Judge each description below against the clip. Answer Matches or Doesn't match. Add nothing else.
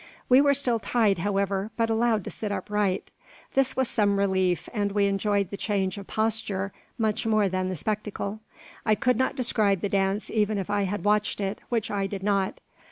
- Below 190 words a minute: Doesn't match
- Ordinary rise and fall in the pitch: Doesn't match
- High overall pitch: Matches